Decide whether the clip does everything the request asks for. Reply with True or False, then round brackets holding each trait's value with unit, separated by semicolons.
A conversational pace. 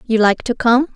False (250 wpm)